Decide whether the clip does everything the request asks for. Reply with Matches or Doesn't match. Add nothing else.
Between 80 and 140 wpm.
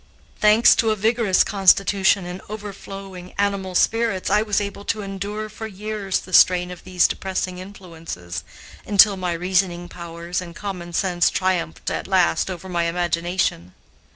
Doesn't match